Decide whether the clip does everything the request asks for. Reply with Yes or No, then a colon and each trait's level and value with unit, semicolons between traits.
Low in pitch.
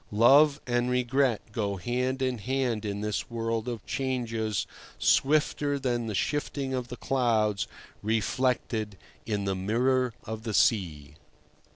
Yes: low, 120 Hz